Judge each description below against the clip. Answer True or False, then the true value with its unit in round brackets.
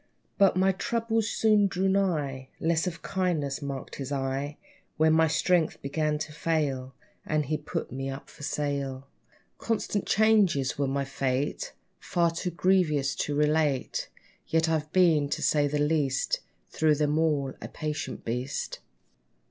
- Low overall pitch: False (150 Hz)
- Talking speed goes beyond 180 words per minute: False (150 wpm)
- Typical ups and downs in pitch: True (3.6 semitones)